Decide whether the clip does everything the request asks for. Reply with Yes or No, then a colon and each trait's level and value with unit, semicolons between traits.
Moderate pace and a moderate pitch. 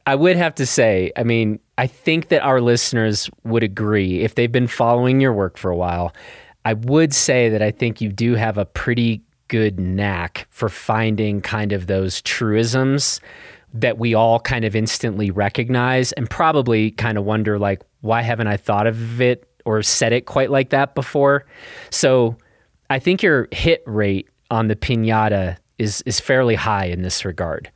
No: average, 180 wpm; low, 115 Hz